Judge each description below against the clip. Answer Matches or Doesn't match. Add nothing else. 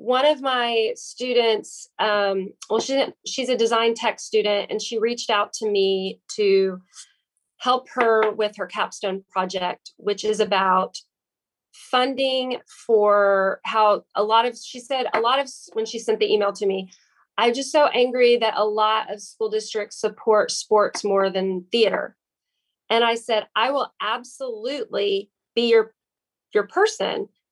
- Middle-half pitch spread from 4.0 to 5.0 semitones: Doesn't match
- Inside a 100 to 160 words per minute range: Matches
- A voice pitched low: Doesn't match